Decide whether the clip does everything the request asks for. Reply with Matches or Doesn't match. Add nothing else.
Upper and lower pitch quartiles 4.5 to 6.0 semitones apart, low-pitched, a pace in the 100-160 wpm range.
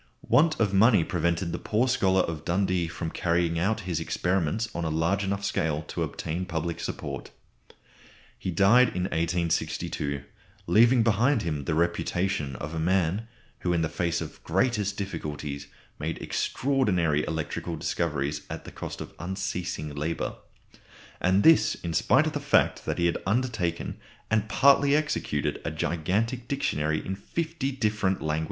Matches